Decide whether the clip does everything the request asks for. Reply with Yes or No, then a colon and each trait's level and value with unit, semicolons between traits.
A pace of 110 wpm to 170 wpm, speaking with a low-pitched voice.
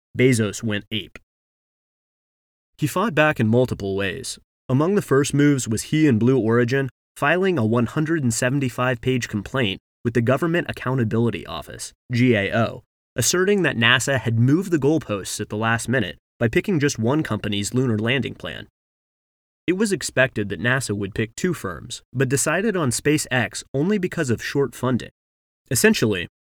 Yes: average, 150 wpm; low, 125 Hz